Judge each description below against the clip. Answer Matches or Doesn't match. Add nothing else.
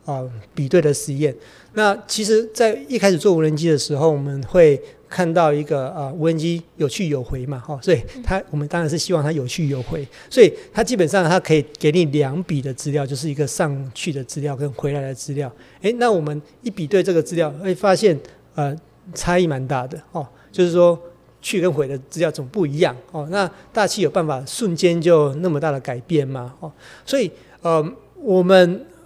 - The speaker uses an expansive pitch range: Doesn't match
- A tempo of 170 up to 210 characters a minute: Doesn't match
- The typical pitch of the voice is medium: Matches